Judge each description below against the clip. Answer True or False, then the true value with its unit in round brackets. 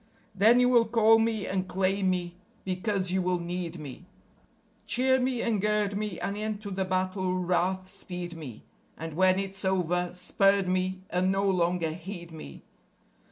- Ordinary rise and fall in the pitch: False (2.2 semitones)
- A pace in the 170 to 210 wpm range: False (160 wpm)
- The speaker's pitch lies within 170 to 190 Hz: True (185 Hz)